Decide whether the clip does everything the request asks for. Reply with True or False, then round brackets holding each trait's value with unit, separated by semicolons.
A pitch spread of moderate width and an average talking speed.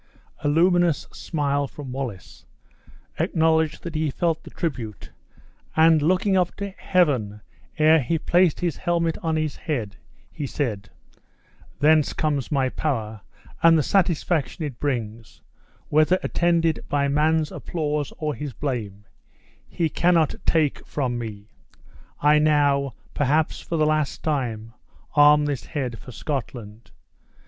False (3.6 semitones; 130 wpm)